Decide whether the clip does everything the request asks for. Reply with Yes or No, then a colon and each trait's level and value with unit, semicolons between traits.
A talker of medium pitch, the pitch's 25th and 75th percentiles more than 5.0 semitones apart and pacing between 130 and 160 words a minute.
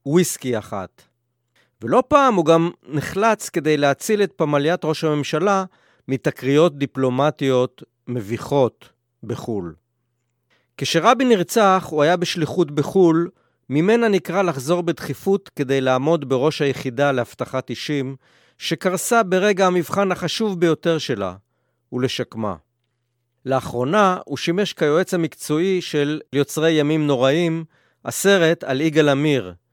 No: medium, 150 Hz; wide, 5.6 semitones; average, 105 wpm